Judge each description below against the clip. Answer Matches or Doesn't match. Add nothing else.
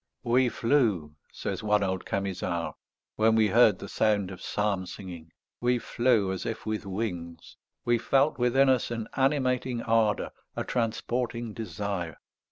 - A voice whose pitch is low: Matches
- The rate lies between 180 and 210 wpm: Doesn't match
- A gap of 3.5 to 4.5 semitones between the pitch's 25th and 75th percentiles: Matches